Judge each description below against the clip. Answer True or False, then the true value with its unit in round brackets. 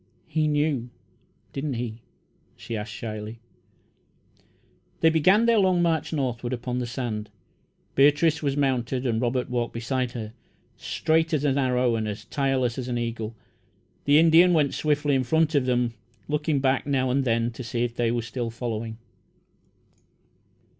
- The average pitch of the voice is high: False (130 Hz)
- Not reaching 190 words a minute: True (155 wpm)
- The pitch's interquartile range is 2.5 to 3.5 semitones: False (3.9 semitones)